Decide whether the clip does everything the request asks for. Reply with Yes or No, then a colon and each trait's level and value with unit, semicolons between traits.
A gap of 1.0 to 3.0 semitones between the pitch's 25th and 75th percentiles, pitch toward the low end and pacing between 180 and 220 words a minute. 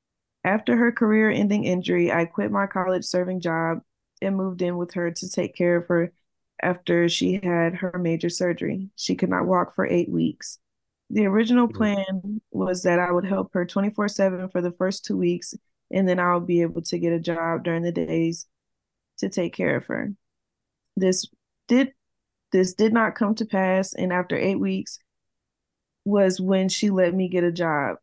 No: narrow, 2.6 semitones; medium, 185 Hz; average, 185 wpm